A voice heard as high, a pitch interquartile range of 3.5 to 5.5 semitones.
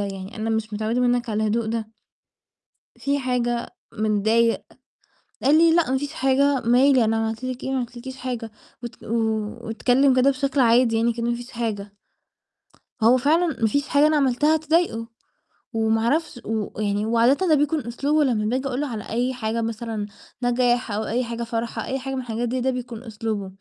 No: high, 240 Hz; average, 3.0 semitones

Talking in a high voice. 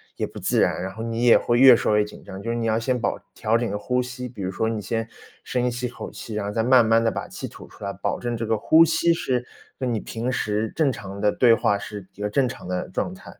No: low, 115 Hz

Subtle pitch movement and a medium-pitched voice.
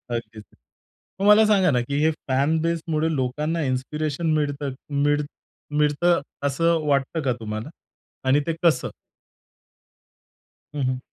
No: average, 3.6 semitones; medium, 150 Hz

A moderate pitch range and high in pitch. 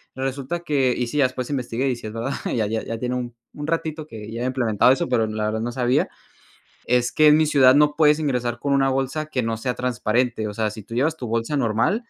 No: average, 3.7 semitones; low, 125 Hz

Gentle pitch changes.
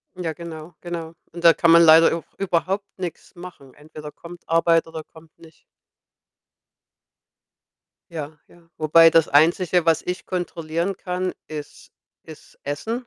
Yes: narrow, 1.8 semitones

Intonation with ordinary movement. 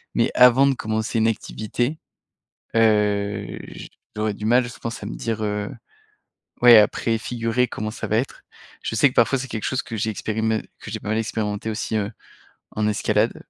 No: narrow, 1.8 semitones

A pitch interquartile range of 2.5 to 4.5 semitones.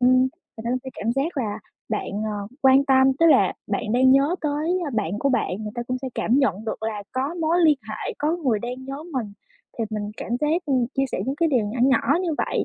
Yes: average, 4.2 semitones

